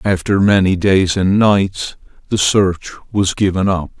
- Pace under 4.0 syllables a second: Yes, 3.7 syllables/s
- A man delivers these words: Yes, male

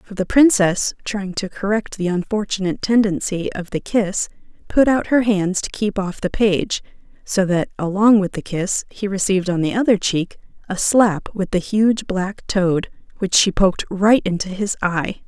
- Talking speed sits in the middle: Yes, average, 185 wpm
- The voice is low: No, high, 195 Hz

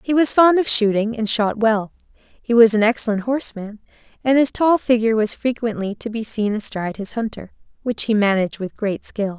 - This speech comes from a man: No, female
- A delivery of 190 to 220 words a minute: Yes, average, 200 wpm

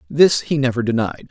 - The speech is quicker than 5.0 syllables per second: Yes, 5.3 syllables/s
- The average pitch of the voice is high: No, low, 130 Hz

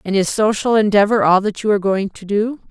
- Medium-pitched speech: No, high, 205 Hz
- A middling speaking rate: No, fast, 245 wpm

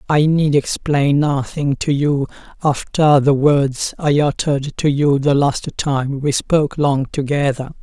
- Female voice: No, male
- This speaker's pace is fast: No, average, 155 wpm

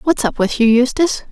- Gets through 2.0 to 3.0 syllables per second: No, 5.7 syllables/s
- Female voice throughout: Yes, female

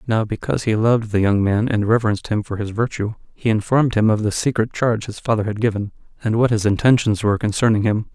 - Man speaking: Yes, male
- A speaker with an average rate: No, fast, 230 wpm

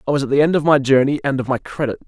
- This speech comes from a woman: No, male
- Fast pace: Yes, fast, 345 wpm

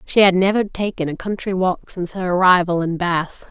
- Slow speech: No, fast, 205 wpm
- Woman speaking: Yes, female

